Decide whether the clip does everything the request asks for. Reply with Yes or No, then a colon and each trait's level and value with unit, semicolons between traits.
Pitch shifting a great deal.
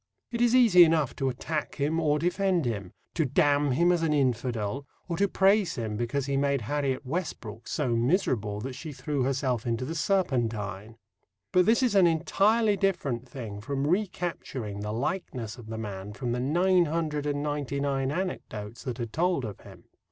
Yes: wide, 6.4 semitones